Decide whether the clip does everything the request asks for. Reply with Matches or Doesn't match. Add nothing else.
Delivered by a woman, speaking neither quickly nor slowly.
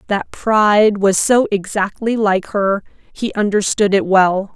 Matches